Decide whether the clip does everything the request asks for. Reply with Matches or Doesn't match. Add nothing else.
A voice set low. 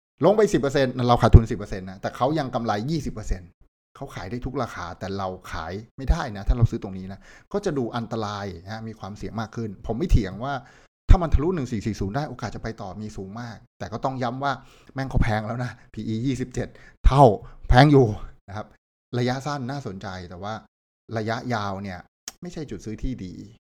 Matches